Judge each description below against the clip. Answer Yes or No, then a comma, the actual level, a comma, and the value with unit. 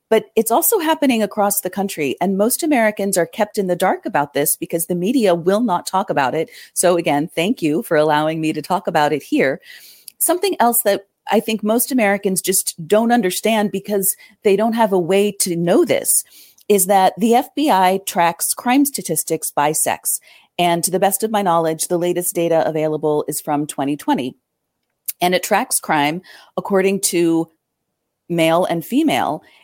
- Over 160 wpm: Yes, average, 180 wpm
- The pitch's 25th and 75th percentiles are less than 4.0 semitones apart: No, average, 4.3 semitones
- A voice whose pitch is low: No, medium, 185 Hz